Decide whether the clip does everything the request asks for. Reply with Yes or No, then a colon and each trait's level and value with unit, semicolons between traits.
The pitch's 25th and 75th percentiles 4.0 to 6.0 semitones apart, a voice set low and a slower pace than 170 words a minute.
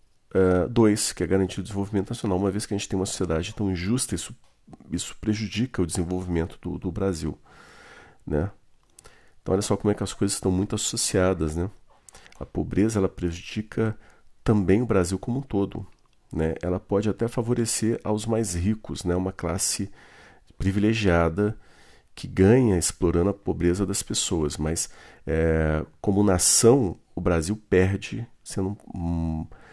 No: average, 3.3 semitones; very low, 95 Hz; average, 155 wpm